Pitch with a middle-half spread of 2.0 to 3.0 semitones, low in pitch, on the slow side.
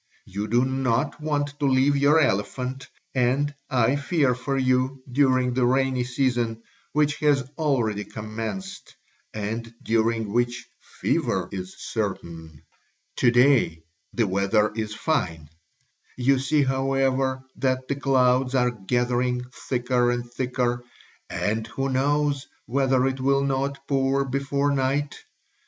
Yes: narrow, 2.6 semitones; low, 130 Hz; slow, 125 wpm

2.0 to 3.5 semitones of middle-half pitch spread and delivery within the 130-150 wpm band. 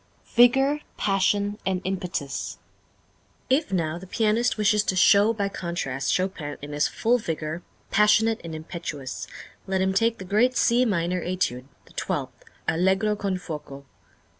No: average, 4.2 semitones; average, 140 wpm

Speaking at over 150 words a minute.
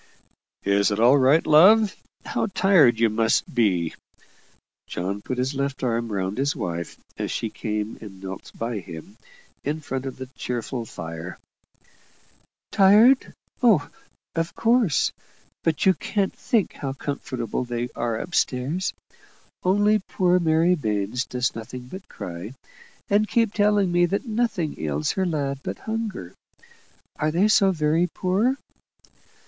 No: average, 140 wpm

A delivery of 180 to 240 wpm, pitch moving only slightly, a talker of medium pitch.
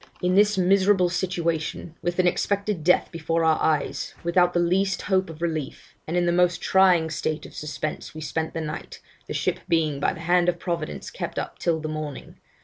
Yes: average, 200 wpm; narrow, 2.3 semitones; medium, 170 Hz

